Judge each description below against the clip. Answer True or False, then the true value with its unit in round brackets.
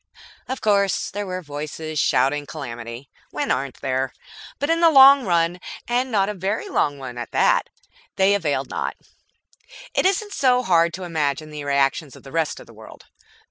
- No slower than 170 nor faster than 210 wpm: True (175 wpm)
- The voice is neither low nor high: True (165 Hz)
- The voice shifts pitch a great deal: True (7.0 semitones)